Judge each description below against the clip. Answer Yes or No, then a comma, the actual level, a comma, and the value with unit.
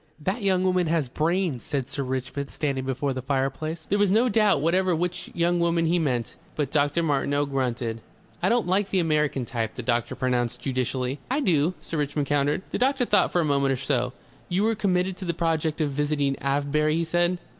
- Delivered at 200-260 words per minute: Yes, fast, 205 wpm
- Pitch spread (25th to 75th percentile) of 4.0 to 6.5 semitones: Yes, average, 4.7 semitones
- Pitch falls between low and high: Yes, medium, 150 Hz